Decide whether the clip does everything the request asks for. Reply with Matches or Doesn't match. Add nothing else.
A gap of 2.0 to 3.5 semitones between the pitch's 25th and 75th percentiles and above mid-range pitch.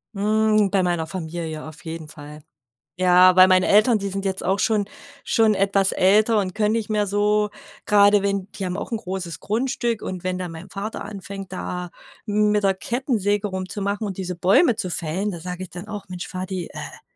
Matches